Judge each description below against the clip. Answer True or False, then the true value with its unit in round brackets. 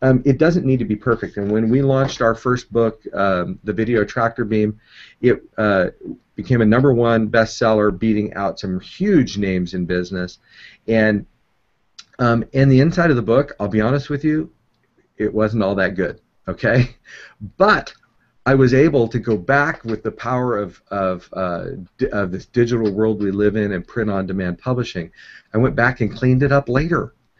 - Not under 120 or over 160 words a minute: False (185 wpm)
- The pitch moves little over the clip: False (3.5 semitones)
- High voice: False (115 Hz)